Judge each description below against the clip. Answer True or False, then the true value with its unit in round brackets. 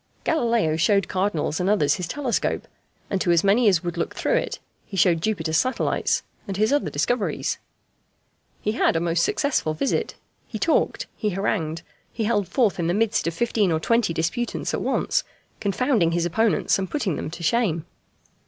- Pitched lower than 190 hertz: False (195 Hz)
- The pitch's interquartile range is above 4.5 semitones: True (5.4 semitones)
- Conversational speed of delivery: True (180 wpm)